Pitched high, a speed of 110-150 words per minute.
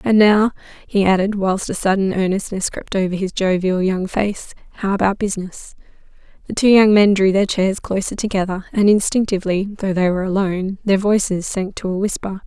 No: high, 195 Hz; average, 185 wpm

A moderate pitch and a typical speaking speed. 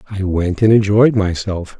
No: low, 100 Hz; average, 165 wpm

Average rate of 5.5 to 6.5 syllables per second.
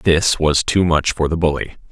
No: 4.8 syllables/s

